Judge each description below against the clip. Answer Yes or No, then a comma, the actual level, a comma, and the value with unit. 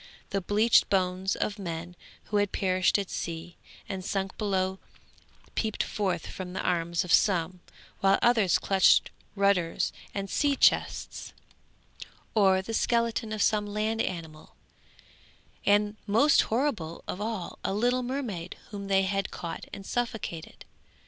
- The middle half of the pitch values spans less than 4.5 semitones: Yes, average, 2.9 semitones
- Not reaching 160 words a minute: Yes, slow, 135 wpm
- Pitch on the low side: No, high, 195 Hz